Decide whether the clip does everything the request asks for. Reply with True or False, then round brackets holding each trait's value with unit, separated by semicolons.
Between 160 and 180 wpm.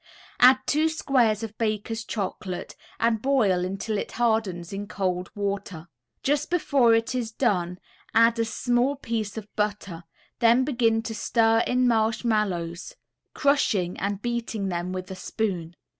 False (145 wpm)